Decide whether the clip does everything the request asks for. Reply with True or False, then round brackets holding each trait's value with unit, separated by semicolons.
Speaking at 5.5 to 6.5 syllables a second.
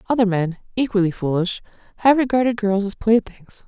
True (5.6 syllables/s)